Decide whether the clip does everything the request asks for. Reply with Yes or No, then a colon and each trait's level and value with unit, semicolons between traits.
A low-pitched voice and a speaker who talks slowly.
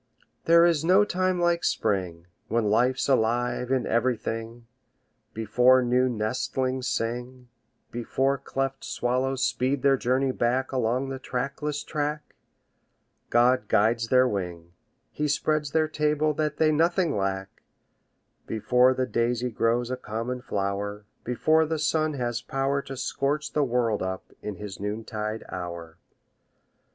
Yes: low, 125 Hz; slow, 130 wpm